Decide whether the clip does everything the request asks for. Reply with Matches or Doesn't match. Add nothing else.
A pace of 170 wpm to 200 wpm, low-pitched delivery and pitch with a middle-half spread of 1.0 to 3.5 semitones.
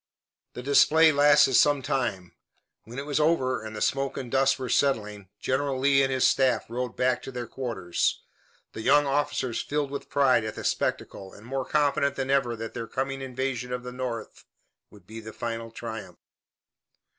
Matches